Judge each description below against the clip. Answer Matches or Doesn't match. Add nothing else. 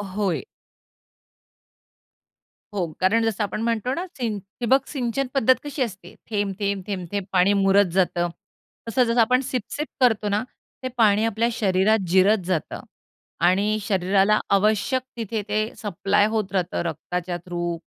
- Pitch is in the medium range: Doesn't match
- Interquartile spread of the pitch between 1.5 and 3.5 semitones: Matches